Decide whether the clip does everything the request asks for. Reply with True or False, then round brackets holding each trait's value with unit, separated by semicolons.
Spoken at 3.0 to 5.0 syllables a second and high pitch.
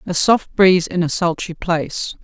False (4.8 syllables/s; 175 Hz)